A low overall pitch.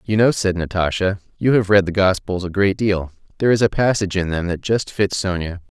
Yes: very low, 95 Hz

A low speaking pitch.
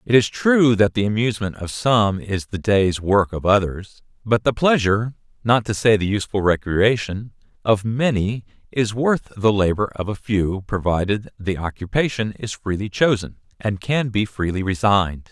Yes: low, 105 Hz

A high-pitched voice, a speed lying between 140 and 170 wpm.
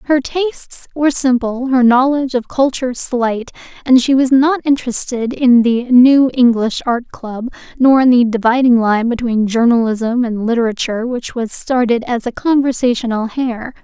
Yes: high, 245 Hz; average, 155 wpm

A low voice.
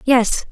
No: high, 240 Hz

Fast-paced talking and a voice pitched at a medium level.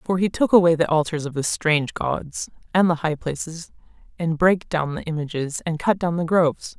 Yes: fast, 210 wpm; medium, 165 Hz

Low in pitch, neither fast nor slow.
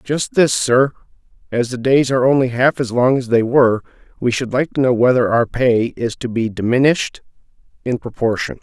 Yes: low, 125 Hz; average, 195 wpm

